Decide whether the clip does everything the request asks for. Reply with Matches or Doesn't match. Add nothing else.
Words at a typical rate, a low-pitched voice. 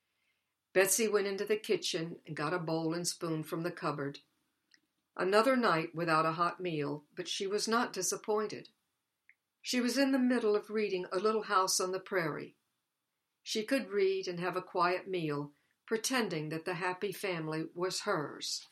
Doesn't match